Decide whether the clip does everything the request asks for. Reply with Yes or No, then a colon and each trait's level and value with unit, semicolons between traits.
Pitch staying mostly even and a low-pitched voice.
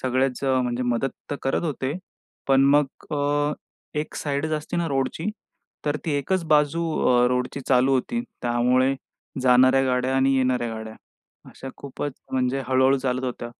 Yes: narrow, 2.2 semitones; low, 130 Hz